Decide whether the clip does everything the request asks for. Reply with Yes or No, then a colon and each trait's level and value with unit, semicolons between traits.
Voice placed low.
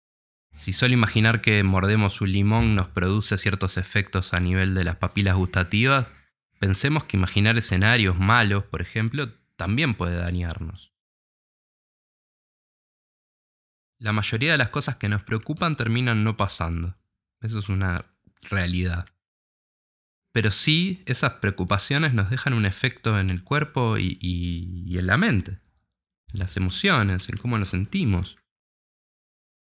Yes: low, 100 Hz